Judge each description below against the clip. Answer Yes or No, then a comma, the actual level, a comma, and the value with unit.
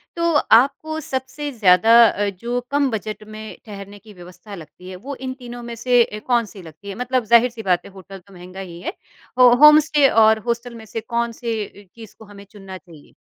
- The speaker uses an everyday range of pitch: Yes, average, 4.1 semitones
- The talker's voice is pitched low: No, high, 220 Hz